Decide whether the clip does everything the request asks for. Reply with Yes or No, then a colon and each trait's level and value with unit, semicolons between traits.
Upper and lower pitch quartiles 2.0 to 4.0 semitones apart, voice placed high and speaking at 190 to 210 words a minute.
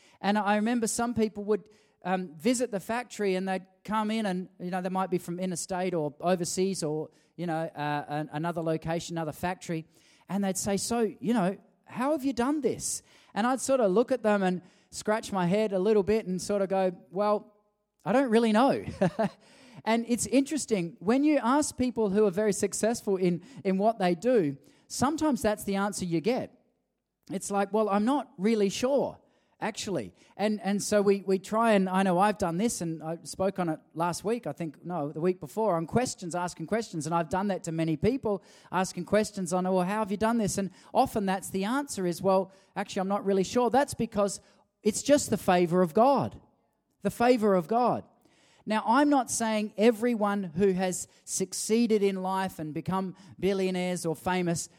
Yes: average, 3.2 semitones; high, 200 Hz; average, 200 wpm